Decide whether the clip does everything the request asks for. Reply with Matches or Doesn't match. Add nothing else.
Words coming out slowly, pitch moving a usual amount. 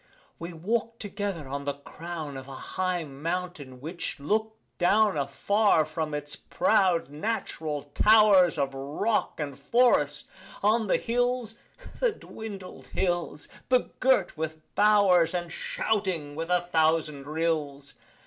Doesn't match